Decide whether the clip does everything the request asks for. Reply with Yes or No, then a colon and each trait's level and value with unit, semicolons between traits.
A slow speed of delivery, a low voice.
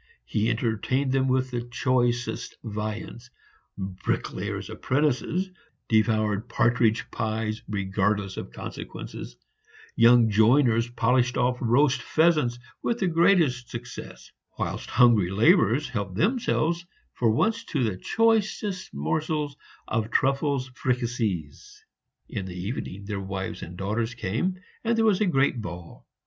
Yes: slow, 120 wpm; low, 120 Hz